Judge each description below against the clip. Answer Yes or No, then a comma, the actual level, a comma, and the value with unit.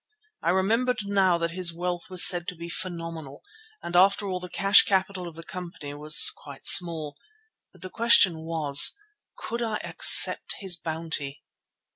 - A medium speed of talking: Yes, average, 155 wpm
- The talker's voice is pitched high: No, medium, 175 Hz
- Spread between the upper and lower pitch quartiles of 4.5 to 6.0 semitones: No, average, 2.9 semitones